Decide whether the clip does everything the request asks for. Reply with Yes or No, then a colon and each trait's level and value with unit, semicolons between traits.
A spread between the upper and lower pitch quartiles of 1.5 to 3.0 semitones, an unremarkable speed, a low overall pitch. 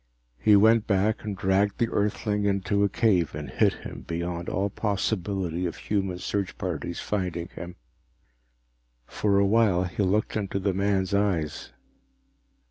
Yes: narrow, 2.5 semitones; average, 145 wpm; low, 100 Hz